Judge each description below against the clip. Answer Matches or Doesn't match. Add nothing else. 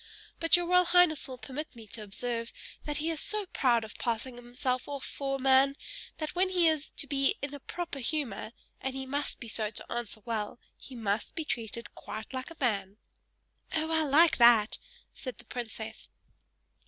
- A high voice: Matches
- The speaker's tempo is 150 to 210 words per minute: Matches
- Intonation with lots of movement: Doesn't match